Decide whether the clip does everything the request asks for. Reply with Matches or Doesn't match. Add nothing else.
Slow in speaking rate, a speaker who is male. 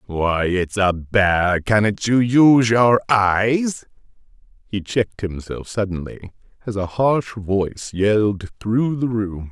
Matches